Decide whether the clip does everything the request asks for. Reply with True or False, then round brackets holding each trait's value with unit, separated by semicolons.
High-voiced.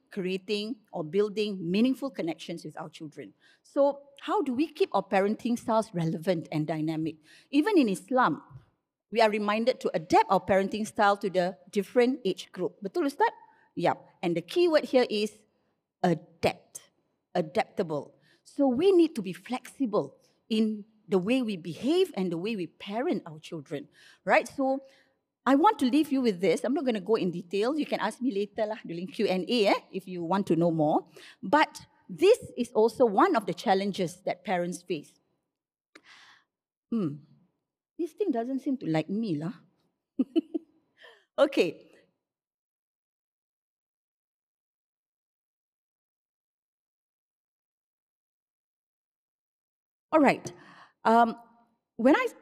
True (215 Hz)